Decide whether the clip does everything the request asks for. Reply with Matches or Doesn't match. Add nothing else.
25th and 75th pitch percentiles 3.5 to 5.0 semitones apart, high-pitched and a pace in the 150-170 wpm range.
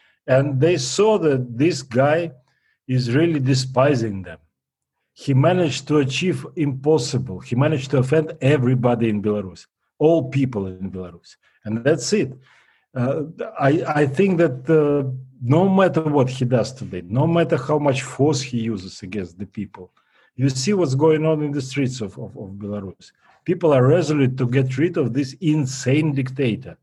Doesn't match